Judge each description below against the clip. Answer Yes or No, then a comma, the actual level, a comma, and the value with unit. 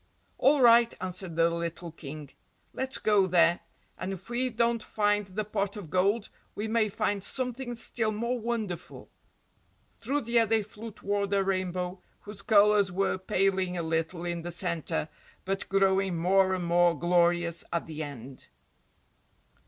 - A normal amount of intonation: Yes, average, 3.8 semitones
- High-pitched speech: Yes, high, 195 Hz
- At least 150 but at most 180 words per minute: Yes, average, 155 wpm